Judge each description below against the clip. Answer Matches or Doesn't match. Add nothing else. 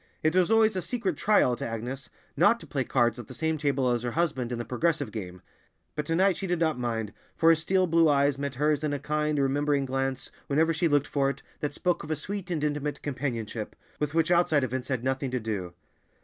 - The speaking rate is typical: Doesn't match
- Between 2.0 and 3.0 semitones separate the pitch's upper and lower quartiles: Doesn't match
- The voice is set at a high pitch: Doesn't match